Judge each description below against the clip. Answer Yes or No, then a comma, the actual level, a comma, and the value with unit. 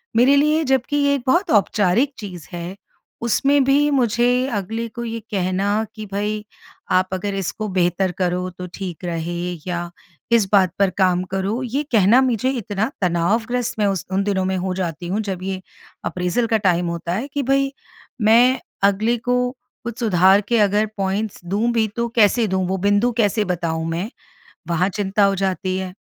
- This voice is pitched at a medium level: No, high, 205 Hz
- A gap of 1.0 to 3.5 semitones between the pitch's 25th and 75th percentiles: No, average, 4.3 semitones